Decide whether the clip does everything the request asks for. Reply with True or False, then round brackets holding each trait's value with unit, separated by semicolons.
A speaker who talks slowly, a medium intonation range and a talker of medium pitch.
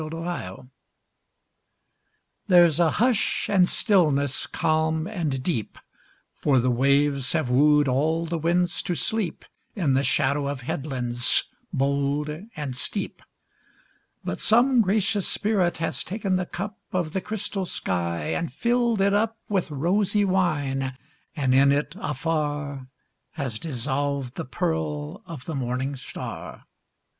True (130 wpm; 5.0 semitones; 155 Hz)